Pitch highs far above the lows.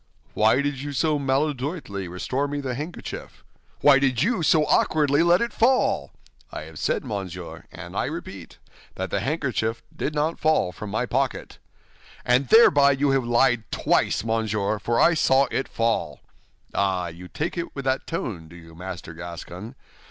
Yes: wide, 6.0 semitones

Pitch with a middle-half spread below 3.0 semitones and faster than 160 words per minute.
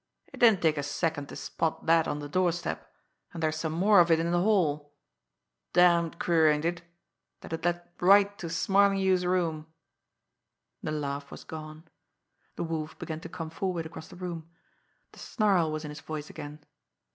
Yes: narrow, 2.4 semitones; average, 180 wpm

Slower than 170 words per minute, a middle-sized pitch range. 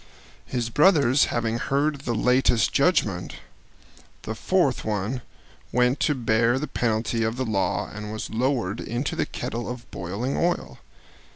Yes: average, 145 wpm; average, 3.0 semitones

